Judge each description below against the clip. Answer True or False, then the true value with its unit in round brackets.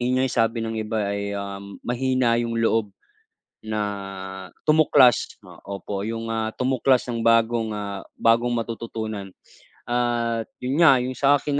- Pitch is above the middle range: False (115 Hz)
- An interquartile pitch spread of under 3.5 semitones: True (2.9 semitones)